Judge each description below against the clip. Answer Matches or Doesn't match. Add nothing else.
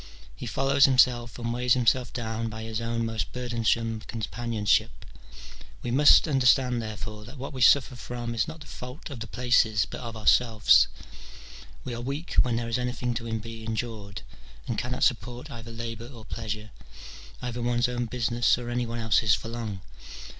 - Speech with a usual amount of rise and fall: Doesn't match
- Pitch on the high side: Doesn't match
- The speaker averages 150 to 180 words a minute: Matches